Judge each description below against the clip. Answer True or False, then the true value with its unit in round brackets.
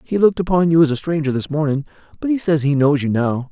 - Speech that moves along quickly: True (275 wpm)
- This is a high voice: False (155 Hz)